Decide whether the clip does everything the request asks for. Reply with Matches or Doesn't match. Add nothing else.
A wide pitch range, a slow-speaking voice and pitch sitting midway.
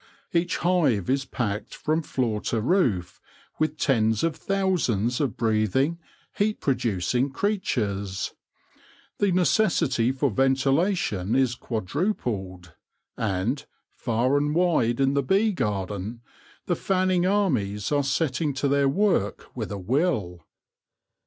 Doesn't match